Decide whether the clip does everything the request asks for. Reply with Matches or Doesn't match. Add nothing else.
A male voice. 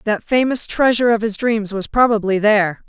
Doesn't match